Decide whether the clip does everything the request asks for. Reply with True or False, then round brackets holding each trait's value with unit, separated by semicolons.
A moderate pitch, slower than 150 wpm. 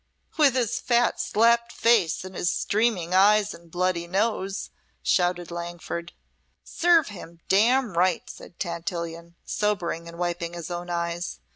True (180 Hz; 135 wpm)